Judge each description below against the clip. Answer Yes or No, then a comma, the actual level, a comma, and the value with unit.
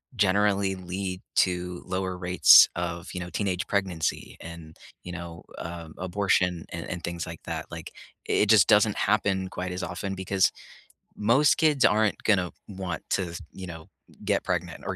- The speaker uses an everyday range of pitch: No, narrow, 2.3 semitones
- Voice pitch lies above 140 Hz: No, very low, 95 Hz